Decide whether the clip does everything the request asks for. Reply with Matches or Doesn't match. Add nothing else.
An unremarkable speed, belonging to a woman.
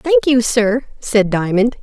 Matches